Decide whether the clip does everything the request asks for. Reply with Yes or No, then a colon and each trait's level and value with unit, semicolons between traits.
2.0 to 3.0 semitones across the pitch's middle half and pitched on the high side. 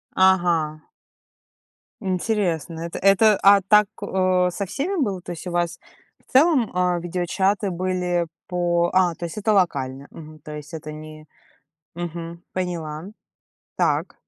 No: narrow, 2.5 semitones; medium, 175 Hz